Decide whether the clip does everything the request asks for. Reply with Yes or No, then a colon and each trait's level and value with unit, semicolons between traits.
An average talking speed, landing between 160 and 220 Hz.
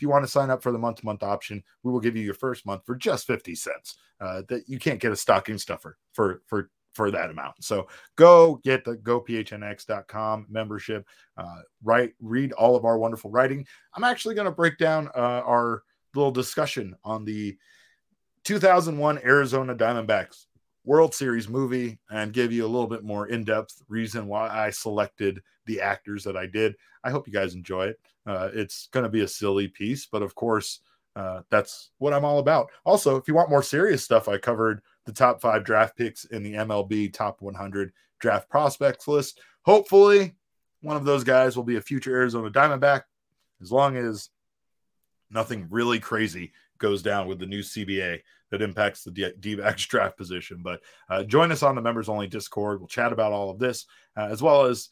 No: average, 190 wpm; low, 115 Hz